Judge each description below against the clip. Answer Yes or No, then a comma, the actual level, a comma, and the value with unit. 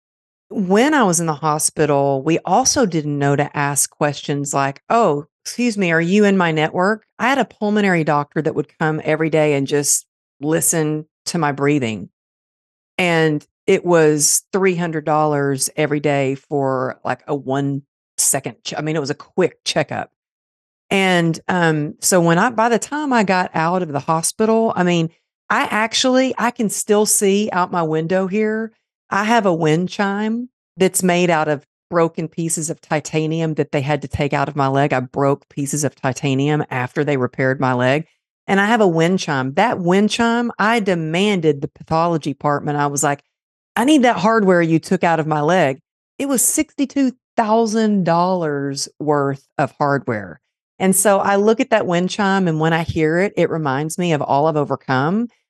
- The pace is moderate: Yes, average, 185 wpm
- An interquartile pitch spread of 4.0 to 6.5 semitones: Yes, average, 5.3 semitones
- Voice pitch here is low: No, medium, 165 Hz